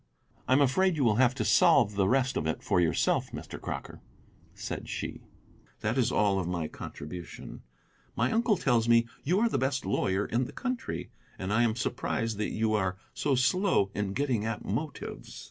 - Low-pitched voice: Yes, low, 115 Hz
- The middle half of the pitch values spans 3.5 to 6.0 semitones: Yes, average, 5.0 semitones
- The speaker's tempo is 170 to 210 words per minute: Yes, average, 190 wpm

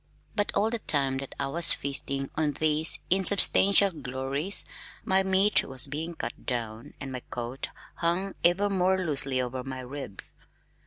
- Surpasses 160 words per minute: No, average, 155 wpm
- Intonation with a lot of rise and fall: Yes, wide, 6.0 semitones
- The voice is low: No, medium, 150 Hz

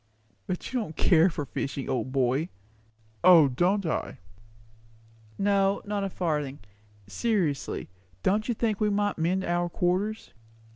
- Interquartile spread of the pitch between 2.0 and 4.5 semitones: No, average, 5.0 semitones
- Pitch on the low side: No, medium, 180 Hz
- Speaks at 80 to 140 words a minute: Yes, slow, 135 wpm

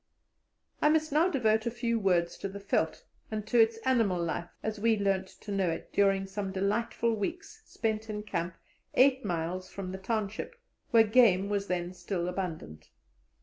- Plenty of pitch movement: No, average, 3.7 semitones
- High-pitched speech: Yes, high, 205 Hz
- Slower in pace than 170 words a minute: No, average, 175 wpm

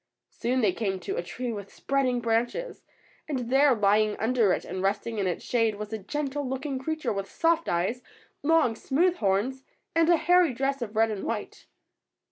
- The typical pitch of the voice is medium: No, high, 240 Hz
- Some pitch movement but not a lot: Yes, average, 4.8 semitones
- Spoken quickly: No, average, 185 wpm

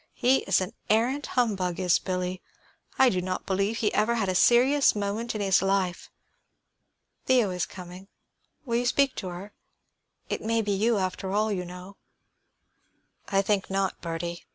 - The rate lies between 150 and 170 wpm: Yes, average, 165 wpm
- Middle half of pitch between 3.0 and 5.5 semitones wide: Yes, average, 3.7 semitones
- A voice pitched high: Yes, high, 195 Hz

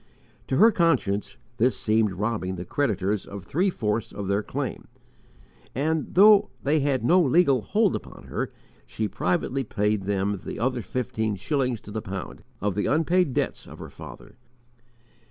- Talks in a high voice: No, low, 115 Hz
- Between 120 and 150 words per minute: No, average, 160 wpm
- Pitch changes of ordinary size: No, wide, 6.2 semitones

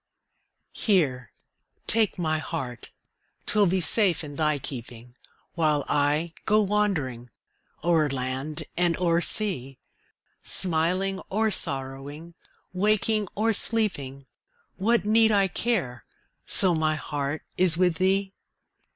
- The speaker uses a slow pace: Yes, slow, 110 wpm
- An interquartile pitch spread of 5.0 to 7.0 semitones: Yes, wide, 5.6 semitones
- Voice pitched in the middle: Yes, medium, 170 Hz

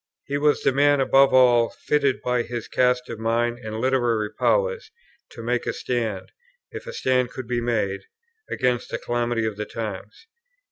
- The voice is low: Yes, low, 120 Hz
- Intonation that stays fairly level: Yes, narrow, 2.3 semitones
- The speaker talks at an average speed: Yes, average, 180 wpm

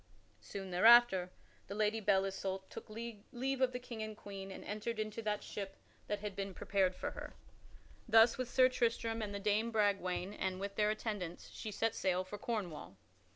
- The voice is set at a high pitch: Yes, high, 210 Hz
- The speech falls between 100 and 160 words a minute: No, average, 190 wpm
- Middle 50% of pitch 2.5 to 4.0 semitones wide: Yes, average, 2.8 semitones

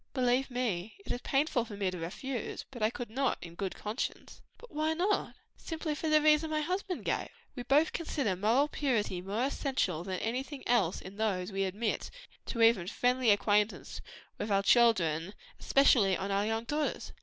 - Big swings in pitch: Yes, wide, 5.7 semitones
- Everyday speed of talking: Yes, average, 170 wpm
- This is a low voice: No, high, 235 Hz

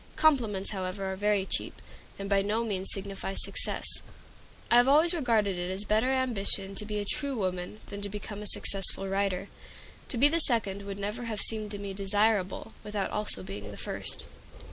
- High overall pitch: Yes, high, 205 Hz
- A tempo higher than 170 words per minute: Yes, average, 190 wpm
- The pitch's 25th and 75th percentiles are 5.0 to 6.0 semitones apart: No, narrow, 2.4 semitones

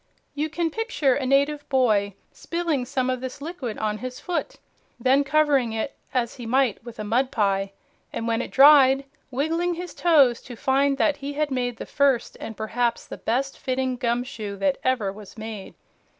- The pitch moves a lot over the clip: No, average, 3.5 semitones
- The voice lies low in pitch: No, very high, 260 Hz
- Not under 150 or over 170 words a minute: No, average, 180 wpm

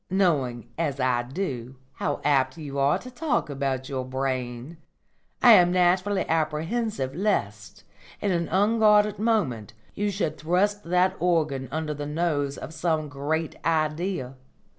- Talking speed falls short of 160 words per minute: Yes, average, 140 wpm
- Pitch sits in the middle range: Yes, medium, 155 Hz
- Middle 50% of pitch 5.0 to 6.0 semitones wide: Yes, average, 5.3 semitones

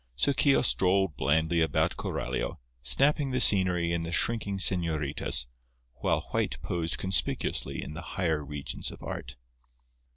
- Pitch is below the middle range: Yes, very low, 85 Hz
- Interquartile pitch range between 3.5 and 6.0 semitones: Yes, average, 4.2 semitones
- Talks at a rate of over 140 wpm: No, slow, 135 wpm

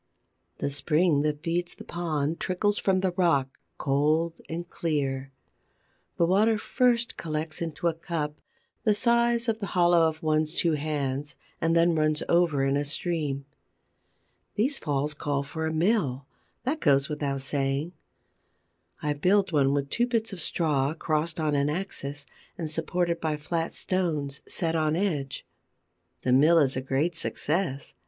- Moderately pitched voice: Yes, medium, 160 Hz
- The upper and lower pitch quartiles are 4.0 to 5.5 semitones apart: No, average, 3.4 semitones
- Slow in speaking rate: No, average, 155 wpm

